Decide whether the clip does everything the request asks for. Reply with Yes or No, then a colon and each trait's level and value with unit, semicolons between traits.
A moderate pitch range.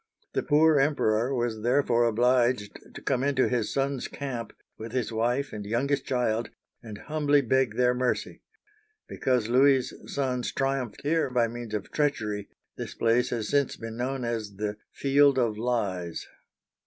Yes: average, 3.3 semitones